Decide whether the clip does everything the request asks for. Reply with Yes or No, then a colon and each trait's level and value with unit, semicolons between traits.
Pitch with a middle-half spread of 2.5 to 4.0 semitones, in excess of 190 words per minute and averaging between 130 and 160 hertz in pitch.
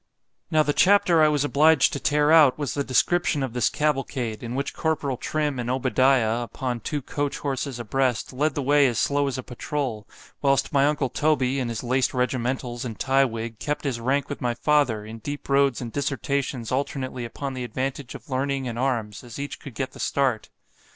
Yes: average, 2.8 semitones; average, 200 wpm; low, 135 Hz